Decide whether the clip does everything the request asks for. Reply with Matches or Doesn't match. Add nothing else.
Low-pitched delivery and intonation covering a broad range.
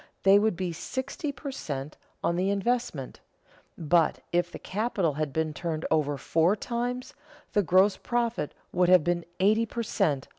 Doesn't match